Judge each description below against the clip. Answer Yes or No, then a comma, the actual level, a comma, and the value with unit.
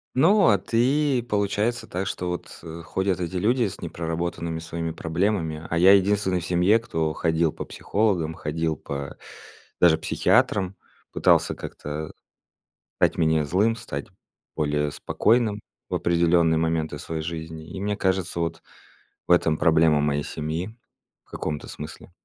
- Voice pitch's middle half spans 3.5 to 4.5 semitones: Yes, average, 3.8 semitones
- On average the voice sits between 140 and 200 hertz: No, very low, 85 Hz